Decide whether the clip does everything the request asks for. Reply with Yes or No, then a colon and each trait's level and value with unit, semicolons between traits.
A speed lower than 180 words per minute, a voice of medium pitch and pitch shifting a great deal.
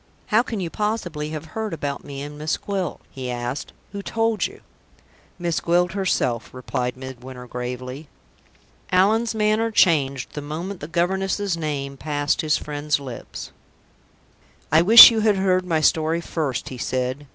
Yes: average, 150 wpm; medium, 155 Hz; wide, 5.7 semitones